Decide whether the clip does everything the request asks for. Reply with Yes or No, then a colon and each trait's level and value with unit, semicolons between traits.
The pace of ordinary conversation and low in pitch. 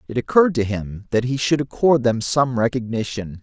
Yes: average, 190 wpm; low, 125 Hz